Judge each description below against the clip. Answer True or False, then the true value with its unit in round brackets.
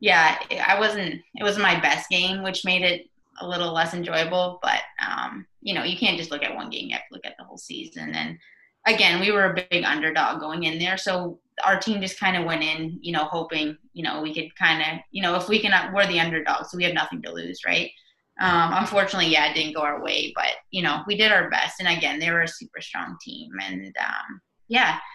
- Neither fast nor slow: False (245 wpm)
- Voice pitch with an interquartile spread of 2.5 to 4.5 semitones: True (3.1 semitones)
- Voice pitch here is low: False (175 Hz)